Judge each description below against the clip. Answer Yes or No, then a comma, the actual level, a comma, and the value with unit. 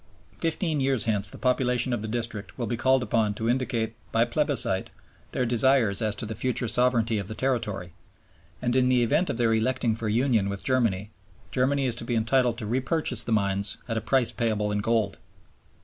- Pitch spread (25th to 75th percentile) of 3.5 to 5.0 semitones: No, average, 2.9 semitones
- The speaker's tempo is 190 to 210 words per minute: Yes, average, 195 wpm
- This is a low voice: Yes, low, 115 Hz